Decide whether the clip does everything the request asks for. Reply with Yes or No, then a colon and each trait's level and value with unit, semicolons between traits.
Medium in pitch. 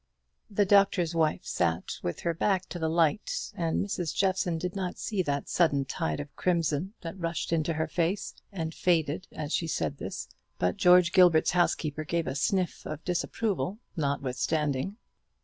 Yes: medium, 165 Hz